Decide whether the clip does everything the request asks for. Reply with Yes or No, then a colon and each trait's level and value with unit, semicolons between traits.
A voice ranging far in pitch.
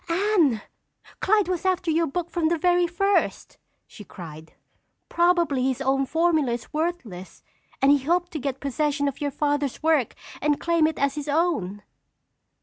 No: average, 4.2 semitones